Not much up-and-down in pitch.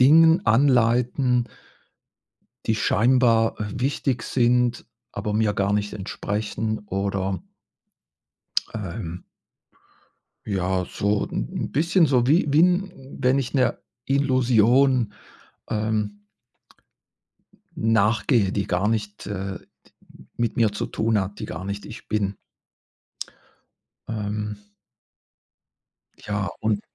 No: average, 3.7 semitones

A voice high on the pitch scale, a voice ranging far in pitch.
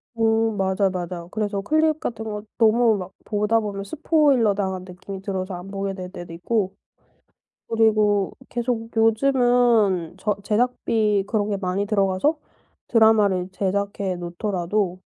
No: high, 205 Hz; average, 3.0 semitones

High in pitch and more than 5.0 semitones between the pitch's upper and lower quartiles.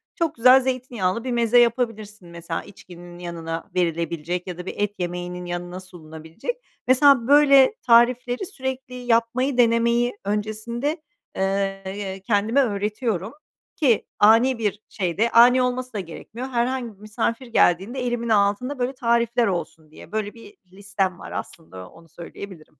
Yes: high, 220 Hz; wide, 5.4 semitones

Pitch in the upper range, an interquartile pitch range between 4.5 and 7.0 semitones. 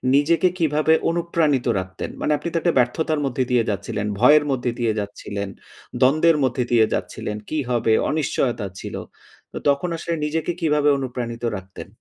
No: low, 135 Hz; average, 5.0 semitones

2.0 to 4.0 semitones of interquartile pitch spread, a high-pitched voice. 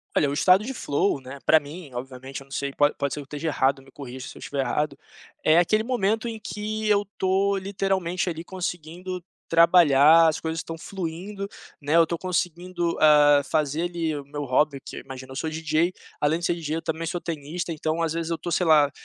No: average, 3.7 semitones; medium, 165 Hz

